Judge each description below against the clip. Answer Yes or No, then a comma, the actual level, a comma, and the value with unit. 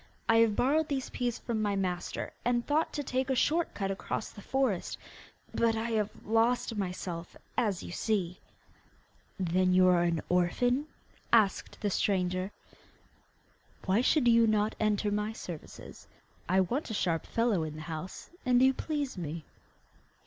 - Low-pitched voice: No, high, 210 Hz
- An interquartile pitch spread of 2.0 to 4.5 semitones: No, average, 5.0 semitones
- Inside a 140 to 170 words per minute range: Yes, average, 155 wpm